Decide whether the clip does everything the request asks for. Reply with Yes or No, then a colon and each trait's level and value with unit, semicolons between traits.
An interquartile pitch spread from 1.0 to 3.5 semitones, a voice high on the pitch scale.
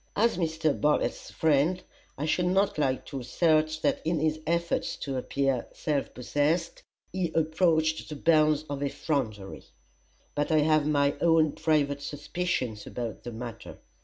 No: narrow, 2.6 semitones; medium, 155 Hz